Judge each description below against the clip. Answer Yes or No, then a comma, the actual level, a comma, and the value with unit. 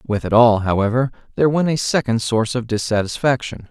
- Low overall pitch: Yes, low, 120 Hz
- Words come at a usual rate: Yes, average, 180 wpm